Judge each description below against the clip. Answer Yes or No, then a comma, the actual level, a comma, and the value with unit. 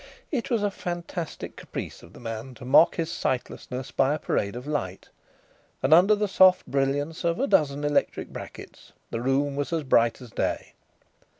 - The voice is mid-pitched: Yes, medium, 145 Hz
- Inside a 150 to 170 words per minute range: No, average, 180 wpm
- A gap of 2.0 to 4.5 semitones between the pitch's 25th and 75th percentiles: No, average, 5.0 semitones